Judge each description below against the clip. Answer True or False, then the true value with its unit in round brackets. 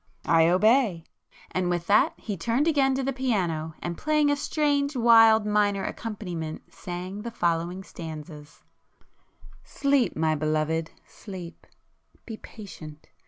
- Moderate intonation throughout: False (6.4 semitones)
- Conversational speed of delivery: False (125 wpm)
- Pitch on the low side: False (195 Hz)